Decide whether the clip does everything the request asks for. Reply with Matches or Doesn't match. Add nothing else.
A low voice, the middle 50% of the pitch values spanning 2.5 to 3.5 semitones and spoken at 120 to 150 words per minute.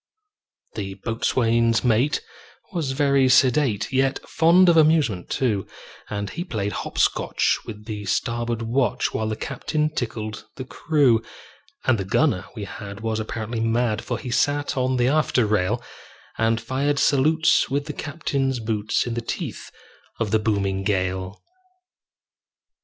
Doesn't match